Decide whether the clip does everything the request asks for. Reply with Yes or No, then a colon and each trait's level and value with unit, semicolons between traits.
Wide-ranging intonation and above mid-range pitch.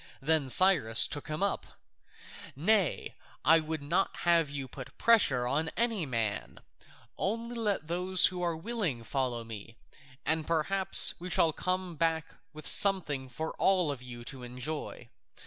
No: wide, 5.7 semitones; medium, 160 Hz